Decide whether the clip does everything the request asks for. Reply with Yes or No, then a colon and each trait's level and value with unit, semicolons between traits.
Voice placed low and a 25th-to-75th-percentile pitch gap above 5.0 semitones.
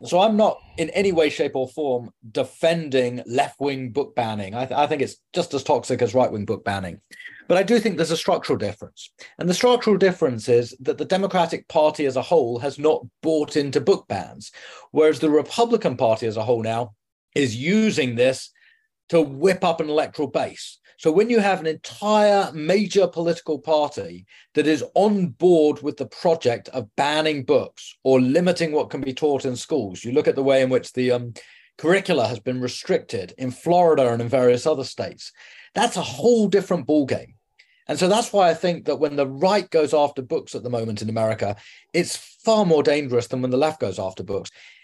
No: medium, 150 Hz; wide, 5.6 semitones